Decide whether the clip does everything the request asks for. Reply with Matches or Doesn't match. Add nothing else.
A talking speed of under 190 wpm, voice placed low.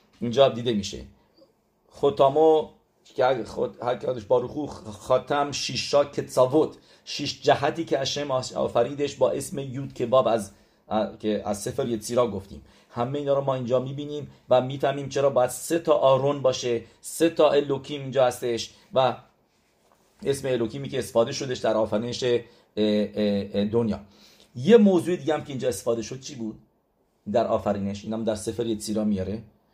Matches